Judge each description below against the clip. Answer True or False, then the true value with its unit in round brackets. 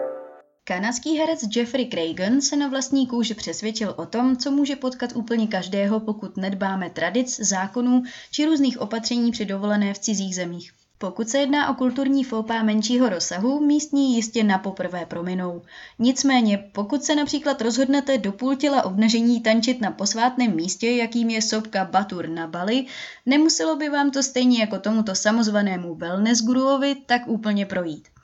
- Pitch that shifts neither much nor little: True (5.0 semitones)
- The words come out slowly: False (155 wpm)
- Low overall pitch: False (230 Hz)